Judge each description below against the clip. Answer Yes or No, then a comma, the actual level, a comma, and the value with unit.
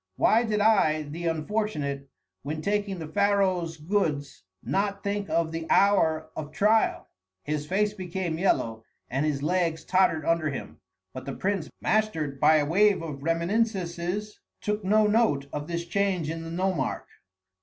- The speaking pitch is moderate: Yes, medium, 170 Hz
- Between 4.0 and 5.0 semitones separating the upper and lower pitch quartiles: Yes, average, 4.6 semitones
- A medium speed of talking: Yes, average, 155 wpm